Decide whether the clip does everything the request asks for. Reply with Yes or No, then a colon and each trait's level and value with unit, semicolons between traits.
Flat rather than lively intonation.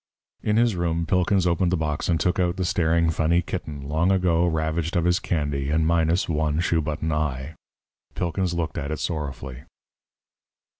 Yes: narrow, 2.2 semitones